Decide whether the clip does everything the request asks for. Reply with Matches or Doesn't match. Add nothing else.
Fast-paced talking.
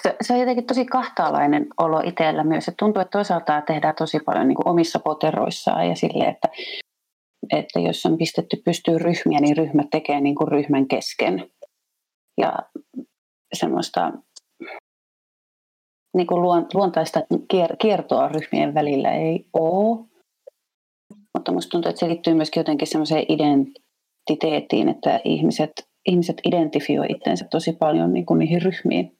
Doesn't match